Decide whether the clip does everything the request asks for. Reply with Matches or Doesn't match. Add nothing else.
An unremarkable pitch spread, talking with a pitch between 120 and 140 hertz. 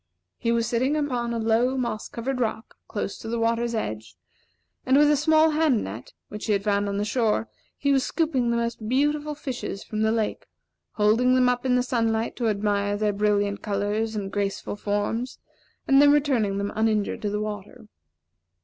Doesn't match